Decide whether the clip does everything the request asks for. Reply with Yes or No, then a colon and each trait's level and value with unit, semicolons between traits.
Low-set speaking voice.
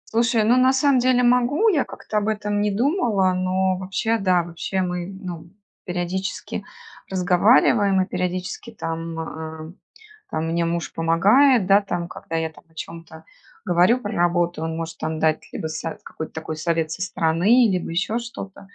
No: medium, 185 Hz